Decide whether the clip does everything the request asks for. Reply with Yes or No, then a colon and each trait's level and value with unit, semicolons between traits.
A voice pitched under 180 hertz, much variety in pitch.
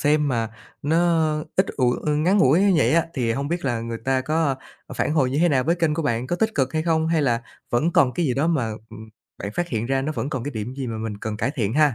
No: medium, 140 Hz; average, 4.9 semitones